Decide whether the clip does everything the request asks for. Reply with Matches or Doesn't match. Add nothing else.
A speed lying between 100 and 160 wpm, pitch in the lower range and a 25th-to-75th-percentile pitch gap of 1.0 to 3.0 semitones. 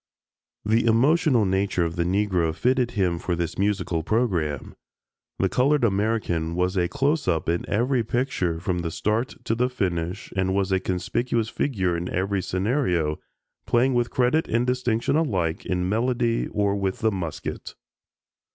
Doesn't match